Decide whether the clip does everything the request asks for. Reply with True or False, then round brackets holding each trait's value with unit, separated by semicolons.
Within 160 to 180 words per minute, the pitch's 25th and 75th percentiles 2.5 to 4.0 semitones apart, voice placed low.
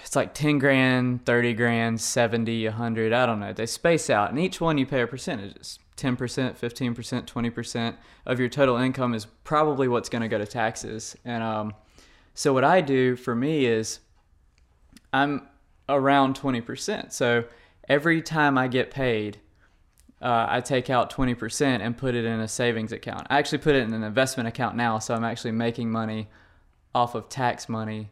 True (175 wpm; 2.8 semitones; 120 Hz)